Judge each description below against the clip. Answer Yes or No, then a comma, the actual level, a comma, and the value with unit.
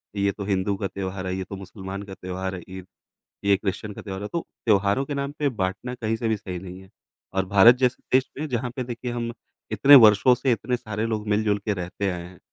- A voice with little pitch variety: No, average, 3.7 semitones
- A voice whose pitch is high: No, low, 105 Hz